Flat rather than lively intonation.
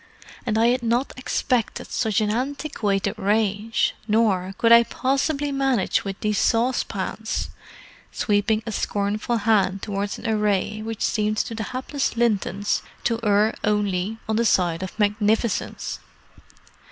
Yes: narrow, 2.3 semitones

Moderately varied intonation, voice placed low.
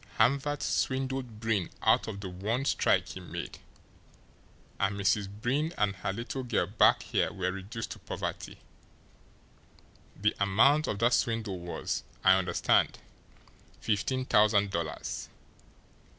Yes: average, 4.5 semitones; low, 105 Hz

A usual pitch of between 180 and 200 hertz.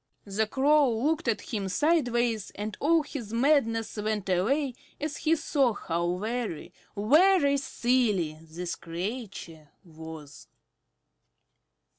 No: high, 225 Hz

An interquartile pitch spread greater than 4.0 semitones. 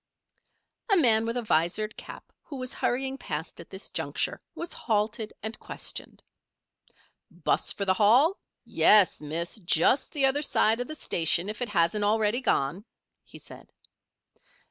Yes: average, 5.1 semitones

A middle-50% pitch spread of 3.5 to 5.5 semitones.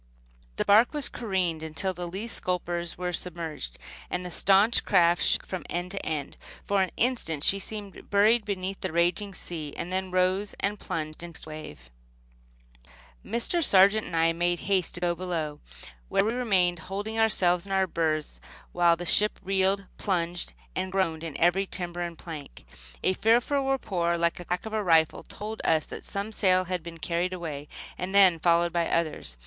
No: average, 2.8 semitones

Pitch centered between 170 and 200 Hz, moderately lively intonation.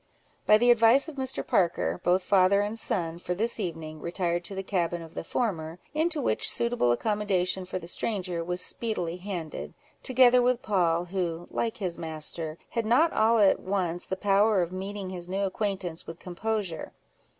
Yes: high, 190 Hz; average, 4.1 semitones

